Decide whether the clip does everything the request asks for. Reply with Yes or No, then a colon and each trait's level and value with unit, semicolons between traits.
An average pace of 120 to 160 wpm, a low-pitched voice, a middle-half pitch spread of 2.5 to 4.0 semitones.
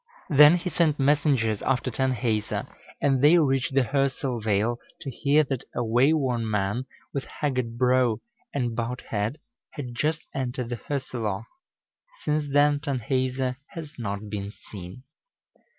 Yes: slow, 135 wpm; low, 130 Hz; average, 3.7 semitones